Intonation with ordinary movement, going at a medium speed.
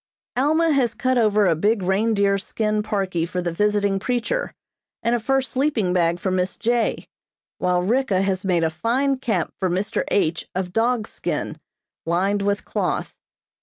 Yes: average, 4.5 semitones; average, 165 wpm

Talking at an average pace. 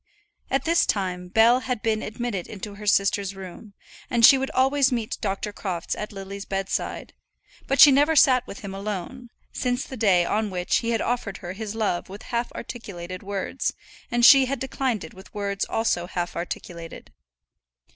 Yes: average, 175 wpm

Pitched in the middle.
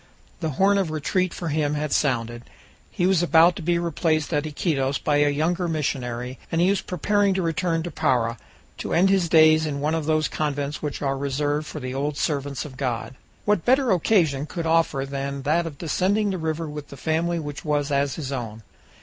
Yes: medium, 155 Hz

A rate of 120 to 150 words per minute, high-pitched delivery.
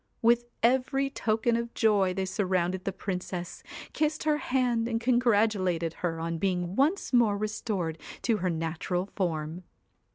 Yes: average, 140 wpm; high, 205 Hz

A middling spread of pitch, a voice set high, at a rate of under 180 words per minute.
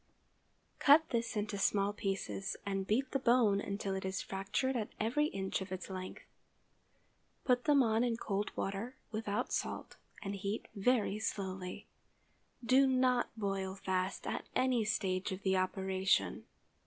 Yes: average, 3.9 semitones; high, 200 Hz; average, 145 wpm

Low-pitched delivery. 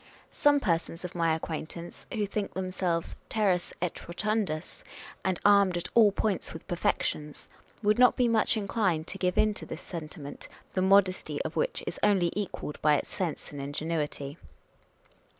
No: medium, 185 Hz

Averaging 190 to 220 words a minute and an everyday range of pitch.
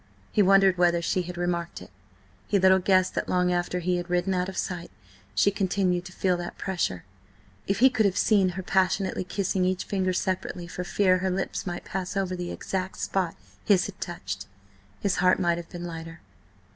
No: average, 195 wpm; narrow, 1.4 semitones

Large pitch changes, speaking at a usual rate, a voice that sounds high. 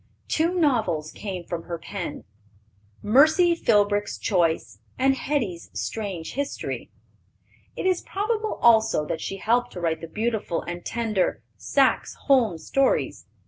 No: wide, 7.8 semitones; slow, 130 wpm; high, 215 Hz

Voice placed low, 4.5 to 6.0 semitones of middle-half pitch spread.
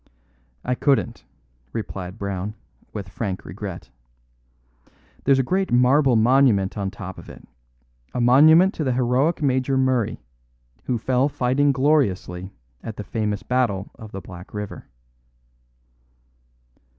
Yes: low, 125 Hz; average, 5.0 semitones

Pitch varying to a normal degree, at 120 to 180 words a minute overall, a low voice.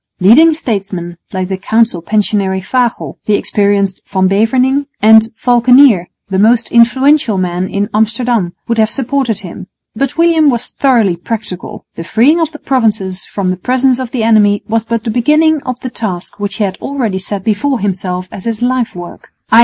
No: average, 4.6 semitones; average, 175 wpm; high, 220 Hz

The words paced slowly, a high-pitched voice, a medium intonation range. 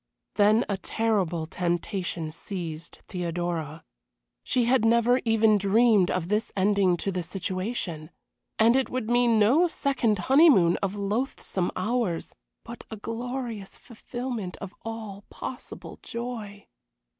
Yes: slow, 120 wpm; high, 210 Hz; average, 4.4 semitones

